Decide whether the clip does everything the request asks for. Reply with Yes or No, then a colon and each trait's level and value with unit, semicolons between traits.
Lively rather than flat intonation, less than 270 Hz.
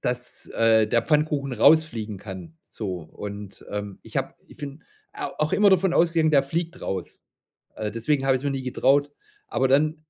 Yes: wide, 6.2 semitones; low, 135 Hz